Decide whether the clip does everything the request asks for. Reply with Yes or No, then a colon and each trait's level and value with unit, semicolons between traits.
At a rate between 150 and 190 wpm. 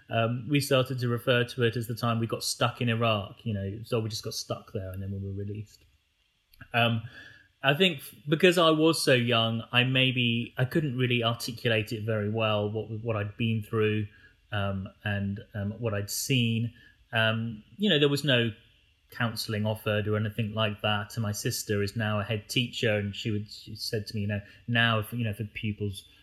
No: fast, 205 wpm